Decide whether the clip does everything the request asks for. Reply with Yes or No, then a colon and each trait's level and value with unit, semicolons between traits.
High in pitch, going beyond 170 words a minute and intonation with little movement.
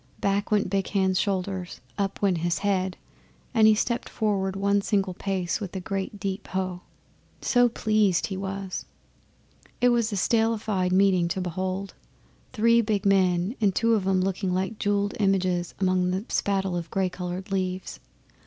No: high, 195 Hz; average, 160 wpm; narrow, 1.7 semitones